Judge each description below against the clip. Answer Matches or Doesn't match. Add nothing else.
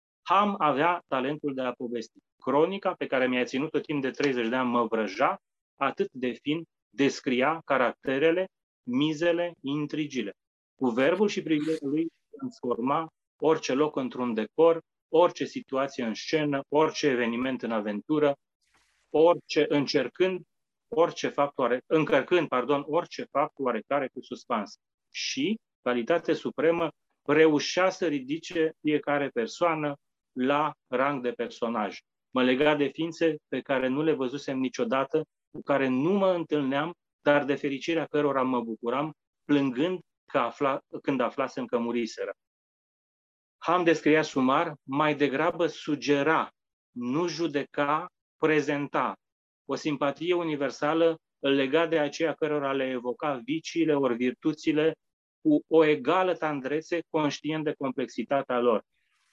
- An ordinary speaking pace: Doesn't match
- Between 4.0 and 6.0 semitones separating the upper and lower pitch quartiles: Doesn't match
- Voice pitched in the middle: Matches